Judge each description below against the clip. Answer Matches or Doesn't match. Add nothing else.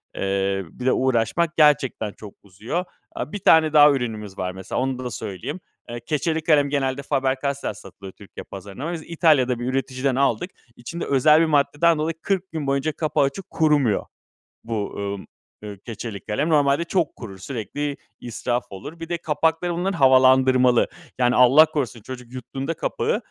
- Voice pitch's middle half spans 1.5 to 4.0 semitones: Doesn't match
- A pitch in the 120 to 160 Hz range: Matches